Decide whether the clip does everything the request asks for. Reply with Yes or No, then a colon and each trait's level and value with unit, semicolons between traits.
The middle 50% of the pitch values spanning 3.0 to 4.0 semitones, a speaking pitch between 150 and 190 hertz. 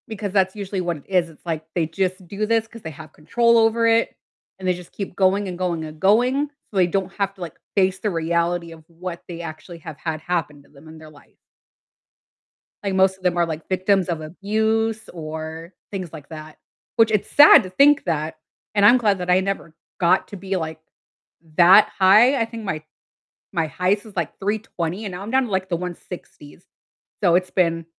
Yes: average, 3.6 semitones; medium, 185 Hz